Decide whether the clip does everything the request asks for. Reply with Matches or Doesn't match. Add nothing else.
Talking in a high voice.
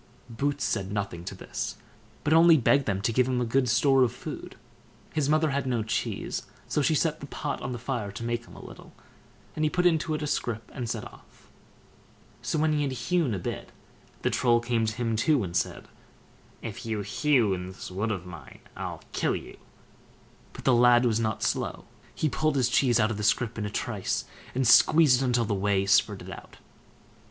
Doesn't match